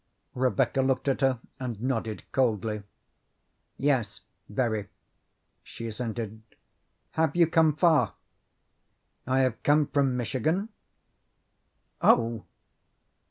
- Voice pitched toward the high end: No, low, 130 Hz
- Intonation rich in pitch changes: No, average, 3.9 semitones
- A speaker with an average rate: No, slow, 95 wpm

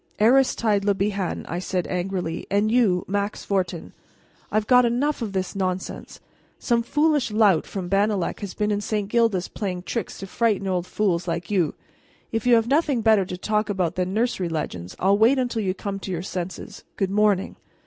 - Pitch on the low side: No, high, 200 Hz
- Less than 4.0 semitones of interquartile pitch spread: Yes, average, 3.3 semitones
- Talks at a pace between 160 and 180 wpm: No, average, 190 wpm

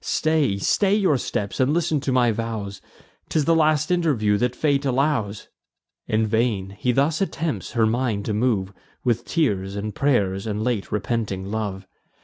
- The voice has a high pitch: No, low, 120 Hz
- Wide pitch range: Yes, wide, 5.8 semitones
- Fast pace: No, average, 160 wpm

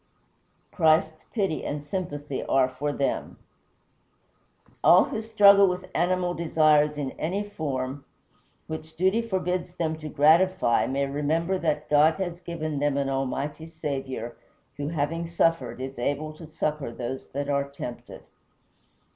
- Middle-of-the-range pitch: Yes, medium, 155 Hz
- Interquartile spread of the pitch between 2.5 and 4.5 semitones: Yes, average, 3.5 semitones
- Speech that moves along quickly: No, slow, 135 wpm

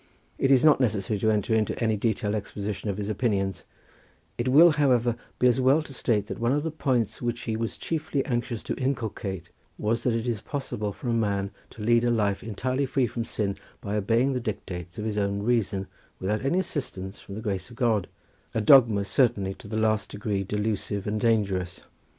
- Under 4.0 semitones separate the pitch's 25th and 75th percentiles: Yes, average, 3.3 semitones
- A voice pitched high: No, low, 110 Hz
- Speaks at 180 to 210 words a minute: Yes, average, 200 wpm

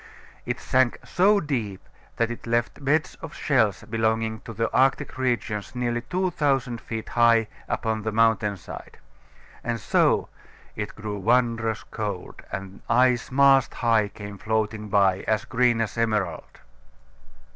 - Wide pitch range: No, narrow, 2.6 semitones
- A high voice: No, low, 115 Hz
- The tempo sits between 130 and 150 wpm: Yes, average, 140 wpm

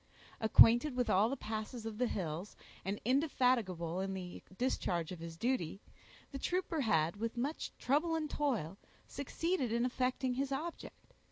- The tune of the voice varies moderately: No, wide, 6.0 semitones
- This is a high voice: Yes, high, 240 Hz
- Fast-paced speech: No, average, 155 wpm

